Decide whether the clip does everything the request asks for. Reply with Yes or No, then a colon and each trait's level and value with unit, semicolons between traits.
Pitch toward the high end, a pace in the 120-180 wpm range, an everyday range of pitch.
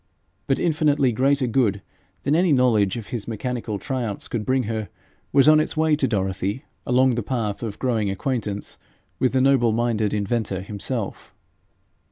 No: low, 120 Hz; average, 160 wpm; average, 4.2 semitones